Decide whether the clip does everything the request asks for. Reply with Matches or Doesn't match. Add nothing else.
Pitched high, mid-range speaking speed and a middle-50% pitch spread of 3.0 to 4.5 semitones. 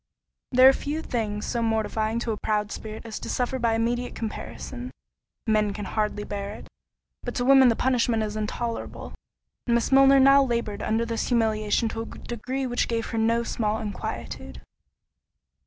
Doesn't match